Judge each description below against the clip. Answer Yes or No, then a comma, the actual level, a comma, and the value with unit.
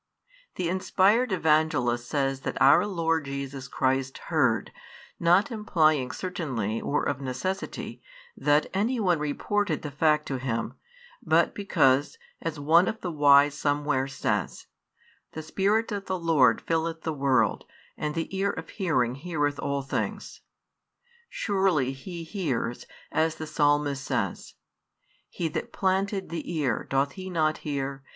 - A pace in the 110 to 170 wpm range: Yes, average, 140 wpm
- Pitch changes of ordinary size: Yes, average, 4.9 semitones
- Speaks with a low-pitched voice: No, medium, 155 Hz